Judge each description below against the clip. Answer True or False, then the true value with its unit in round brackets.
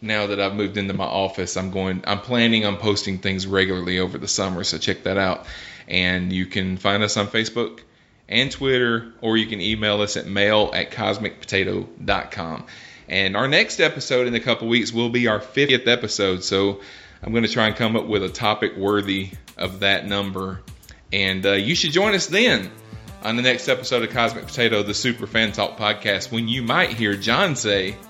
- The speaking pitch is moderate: False (105 Hz)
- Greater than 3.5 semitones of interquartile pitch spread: False (3.1 semitones)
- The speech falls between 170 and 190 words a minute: False (200 wpm)